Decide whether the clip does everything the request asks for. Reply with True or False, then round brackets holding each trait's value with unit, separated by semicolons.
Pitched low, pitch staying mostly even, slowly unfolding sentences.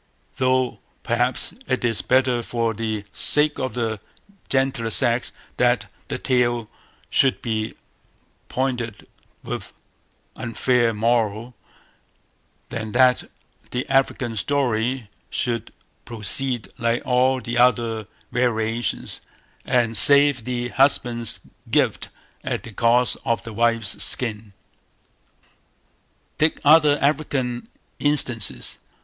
True (120 Hz; 2.2 semitones; 105 wpm)